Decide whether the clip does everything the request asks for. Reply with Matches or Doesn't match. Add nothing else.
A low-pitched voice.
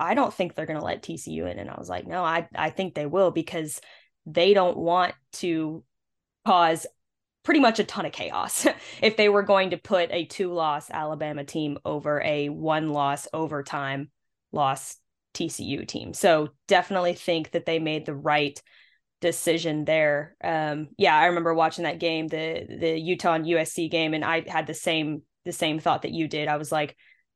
Doesn't match